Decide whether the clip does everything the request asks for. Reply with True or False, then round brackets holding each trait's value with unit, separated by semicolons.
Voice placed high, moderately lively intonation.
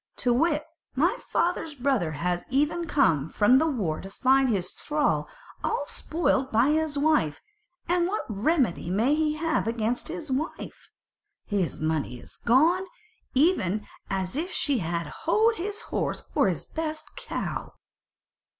False (270 Hz; 7.9 semitones)